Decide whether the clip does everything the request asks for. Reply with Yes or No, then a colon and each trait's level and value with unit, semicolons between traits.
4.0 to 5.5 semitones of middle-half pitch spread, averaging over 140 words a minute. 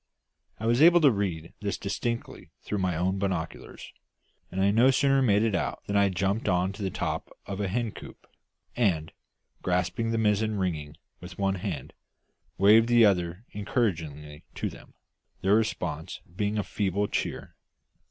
No: average, 3.6 semitones; average, 160 wpm